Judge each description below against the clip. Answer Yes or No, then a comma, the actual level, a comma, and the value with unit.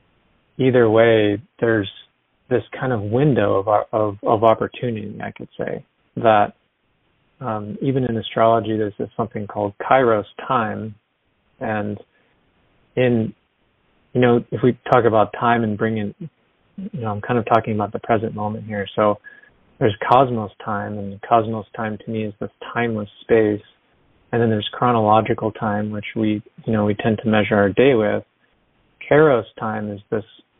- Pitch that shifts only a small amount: Yes, narrow, 2.1 semitones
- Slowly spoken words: No, average, 160 wpm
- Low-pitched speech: Yes, low, 110 Hz